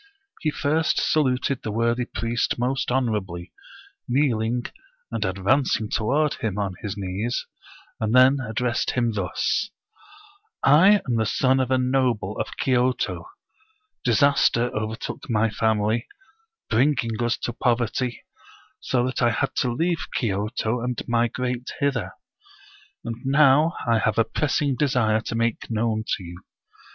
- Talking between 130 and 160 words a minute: Yes, average, 140 wpm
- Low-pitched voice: Yes, low, 120 Hz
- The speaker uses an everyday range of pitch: Yes, average, 3.3 semitones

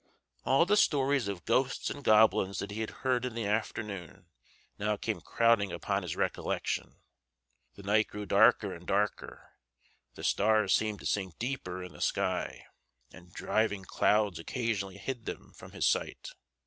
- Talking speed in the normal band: Yes, average, 160 wpm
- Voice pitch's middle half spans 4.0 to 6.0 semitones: No, average, 3.0 semitones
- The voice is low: Yes, low, 105 Hz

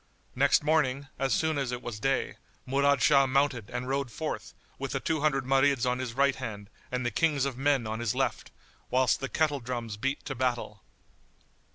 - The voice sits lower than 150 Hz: Yes, low, 135 Hz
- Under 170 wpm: No, average, 195 wpm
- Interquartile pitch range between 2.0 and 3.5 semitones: Yes, narrow, 2.4 semitones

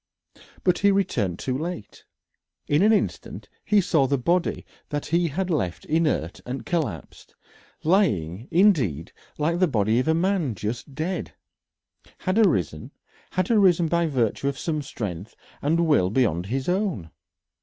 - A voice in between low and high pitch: Yes, medium, 150 Hz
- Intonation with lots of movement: Yes, wide, 8.2 semitones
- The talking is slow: No, average, 145 wpm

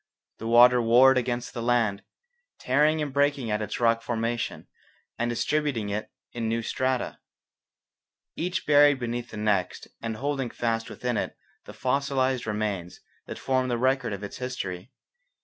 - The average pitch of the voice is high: No, low, 120 Hz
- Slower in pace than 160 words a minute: Yes, average, 150 wpm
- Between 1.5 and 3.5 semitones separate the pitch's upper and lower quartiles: Yes, average, 2.8 semitones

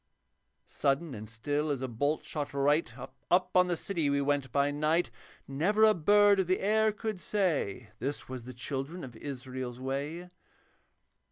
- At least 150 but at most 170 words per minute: Yes, average, 165 wpm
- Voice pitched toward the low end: No, medium, 145 Hz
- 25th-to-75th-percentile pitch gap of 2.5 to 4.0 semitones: No, average, 5.2 semitones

